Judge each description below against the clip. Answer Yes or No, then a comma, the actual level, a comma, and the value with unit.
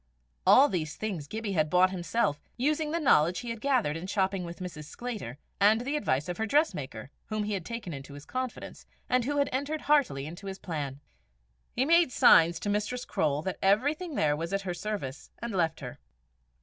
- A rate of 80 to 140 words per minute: No, average, 200 wpm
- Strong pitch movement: Yes, wide, 7.8 semitones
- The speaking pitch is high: Yes, high, 195 Hz